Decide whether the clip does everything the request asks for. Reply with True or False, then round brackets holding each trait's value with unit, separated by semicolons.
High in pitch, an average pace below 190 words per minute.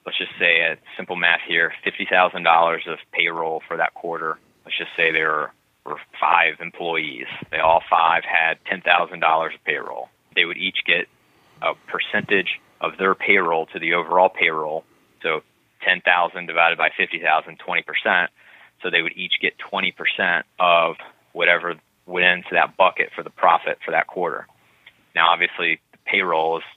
False (80 Hz; 155 wpm)